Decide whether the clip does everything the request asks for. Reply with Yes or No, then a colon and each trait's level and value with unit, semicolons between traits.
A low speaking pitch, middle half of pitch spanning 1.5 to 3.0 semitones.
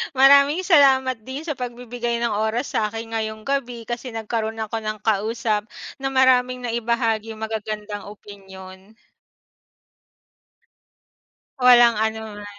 No: high, 230 Hz; narrow, 2.6 semitones